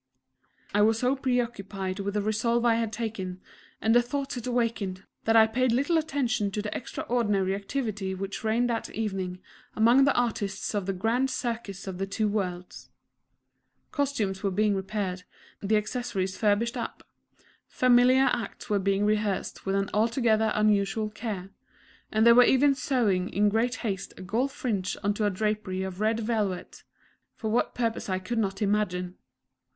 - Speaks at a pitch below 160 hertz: No, high, 215 Hz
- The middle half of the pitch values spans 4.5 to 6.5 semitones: No, average, 3.3 semitones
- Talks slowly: No, average, 165 wpm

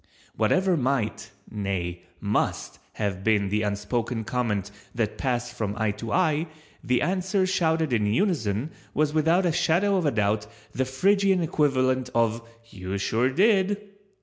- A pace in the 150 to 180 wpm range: No, average, 140 wpm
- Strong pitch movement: Yes, wide, 8.1 semitones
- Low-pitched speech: Yes, low, 125 Hz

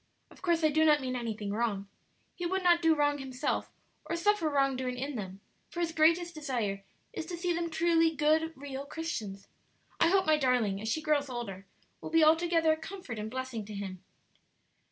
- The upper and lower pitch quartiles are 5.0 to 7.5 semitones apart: Yes, wide, 5.5 semitones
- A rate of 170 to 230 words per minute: Yes, average, 195 wpm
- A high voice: Yes, very high, 295 Hz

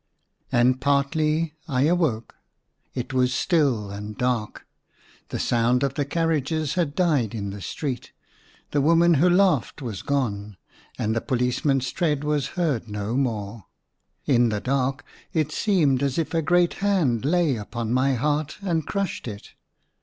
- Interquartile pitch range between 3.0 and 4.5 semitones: No, average, 4.9 semitones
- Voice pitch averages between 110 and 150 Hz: Yes, medium, 140 Hz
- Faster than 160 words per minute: No, average, 150 wpm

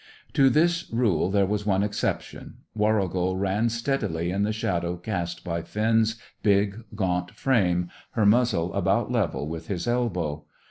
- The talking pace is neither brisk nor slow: Yes, average, 145 wpm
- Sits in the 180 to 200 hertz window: No, low, 100 Hz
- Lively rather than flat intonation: No, average, 4.1 semitones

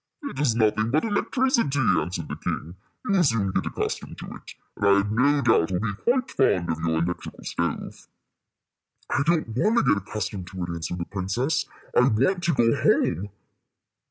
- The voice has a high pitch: No, low, 110 Hz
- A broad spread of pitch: Yes, wide, 8.0 semitones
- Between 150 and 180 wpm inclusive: No, average, 190 wpm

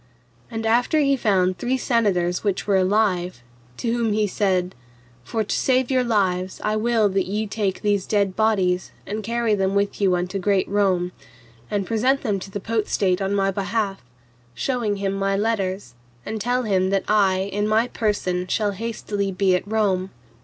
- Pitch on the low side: No, high, 205 Hz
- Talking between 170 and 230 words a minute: Yes, average, 175 wpm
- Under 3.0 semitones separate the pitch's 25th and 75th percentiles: Yes, narrow, 2.6 semitones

